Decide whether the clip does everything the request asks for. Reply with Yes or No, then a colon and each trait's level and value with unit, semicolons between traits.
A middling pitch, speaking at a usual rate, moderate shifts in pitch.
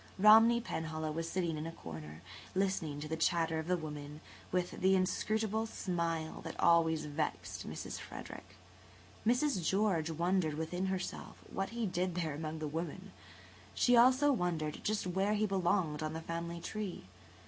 Yes: medium, 170 Hz; average, 160 wpm; average, 3.5 semitones